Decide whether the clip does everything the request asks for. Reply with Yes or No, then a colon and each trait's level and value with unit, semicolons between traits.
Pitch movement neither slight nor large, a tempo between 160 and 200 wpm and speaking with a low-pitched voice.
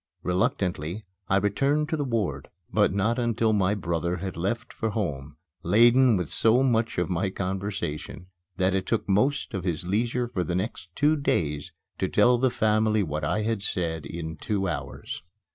Yes: average, 4.8 semitones; average, 175 wpm; low, 100 Hz